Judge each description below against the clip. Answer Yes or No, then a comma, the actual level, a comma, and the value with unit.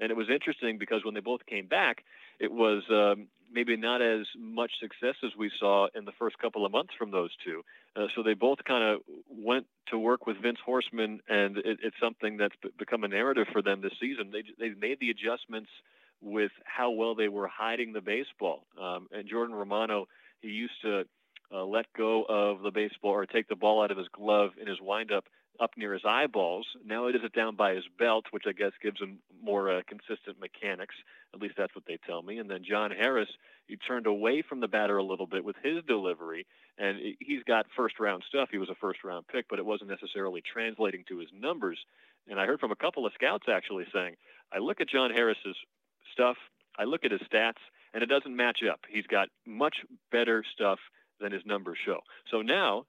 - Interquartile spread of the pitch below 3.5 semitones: Yes, narrow, 2.4 semitones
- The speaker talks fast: Yes, fast, 220 wpm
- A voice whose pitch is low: Yes, low, 110 Hz